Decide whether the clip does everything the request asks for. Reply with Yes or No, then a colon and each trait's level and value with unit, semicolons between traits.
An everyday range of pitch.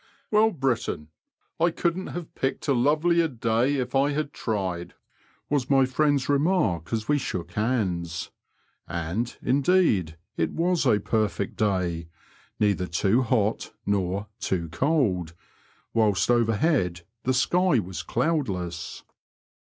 No: wide, 7.9 semitones